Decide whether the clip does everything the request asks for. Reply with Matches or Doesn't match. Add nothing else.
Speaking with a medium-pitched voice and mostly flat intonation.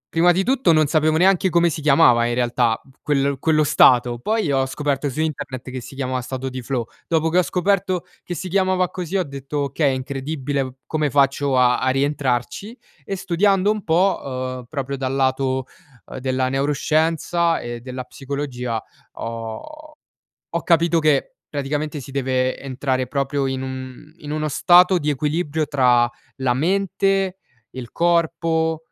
Doesn't match